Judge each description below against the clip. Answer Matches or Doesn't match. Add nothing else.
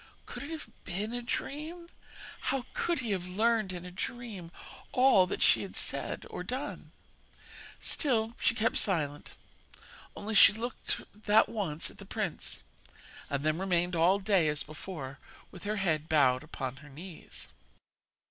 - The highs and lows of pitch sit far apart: Matches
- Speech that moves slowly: Doesn't match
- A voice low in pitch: Doesn't match